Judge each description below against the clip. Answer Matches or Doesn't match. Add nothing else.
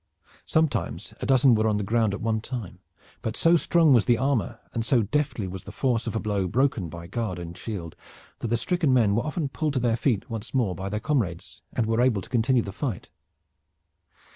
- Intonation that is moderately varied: Matches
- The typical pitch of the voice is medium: Doesn't match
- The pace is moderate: Doesn't match